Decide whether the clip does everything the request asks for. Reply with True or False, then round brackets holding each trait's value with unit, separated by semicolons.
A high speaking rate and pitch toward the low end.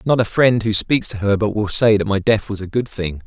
True (310 wpm; 105 Hz)